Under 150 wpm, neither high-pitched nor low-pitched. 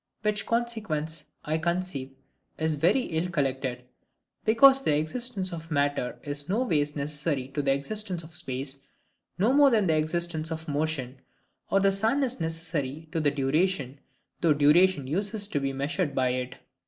No: average, 155 wpm; medium, 160 Hz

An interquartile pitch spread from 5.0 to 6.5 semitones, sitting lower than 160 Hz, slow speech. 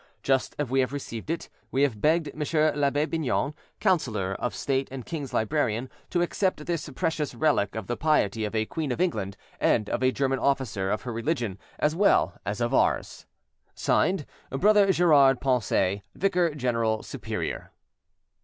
No: wide, 5.5 semitones; low, 135 Hz; average, 165 wpm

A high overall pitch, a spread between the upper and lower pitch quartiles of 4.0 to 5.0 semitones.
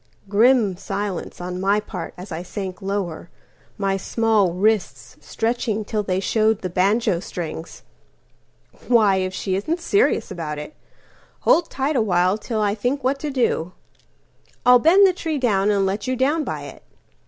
Yes: high, 205 Hz; average, 4.7 semitones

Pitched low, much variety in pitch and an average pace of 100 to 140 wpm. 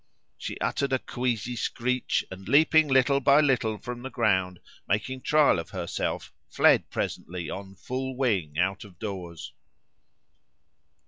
Yes: low, 120 Hz; wide, 5.7 semitones; slow, 135 wpm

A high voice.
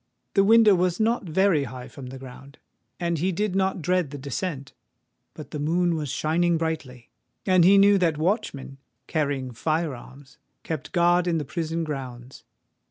No: medium, 160 Hz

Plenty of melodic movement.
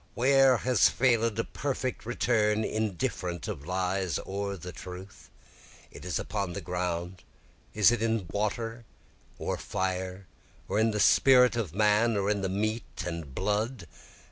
No: average, 3.8 semitones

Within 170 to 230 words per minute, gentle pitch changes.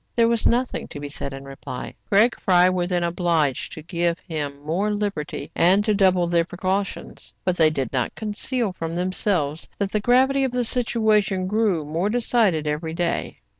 No: average, 180 wpm; average, 4.7 semitones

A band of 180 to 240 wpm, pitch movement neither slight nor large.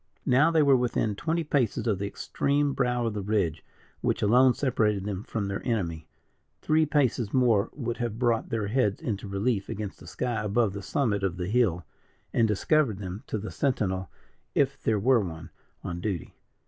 Yes: average, 185 wpm; average, 4.2 semitones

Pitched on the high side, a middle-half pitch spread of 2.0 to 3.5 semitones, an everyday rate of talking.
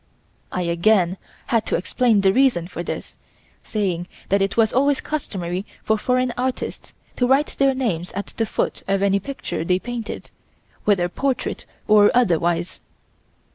No: high, 205 Hz; wide, 5.6 semitones; average, 150 wpm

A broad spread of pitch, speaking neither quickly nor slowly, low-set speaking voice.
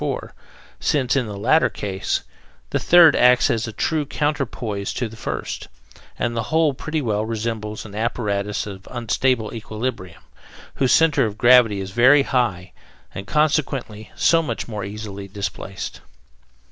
No: average, 4.2 semitones; average, 150 wpm; low, 115 Hz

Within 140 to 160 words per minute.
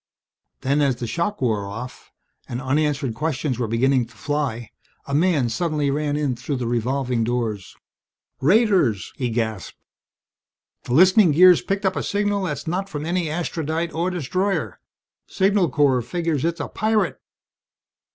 Yes: average, 150 wpm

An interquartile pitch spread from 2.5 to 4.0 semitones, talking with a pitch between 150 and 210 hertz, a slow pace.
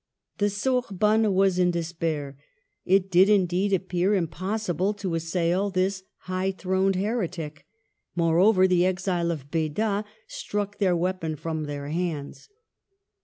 Yes: average, 2.9 semitones; medium, 185 Hz; slow, 120 wpm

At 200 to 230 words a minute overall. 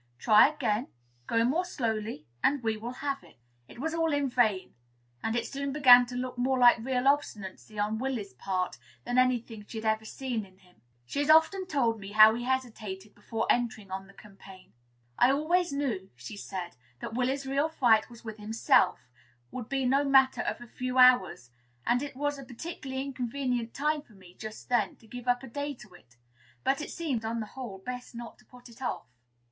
Yes: fast, 205 wpm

